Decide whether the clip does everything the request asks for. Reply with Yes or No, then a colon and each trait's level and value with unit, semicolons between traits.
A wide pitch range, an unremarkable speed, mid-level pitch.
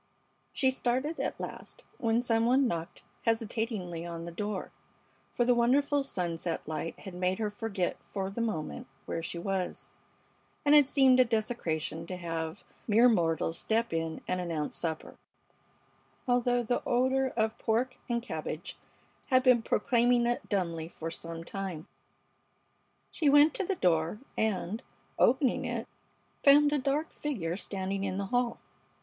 No: wide, 6.3 semitones; average, 150 wpm; high, 220 Hz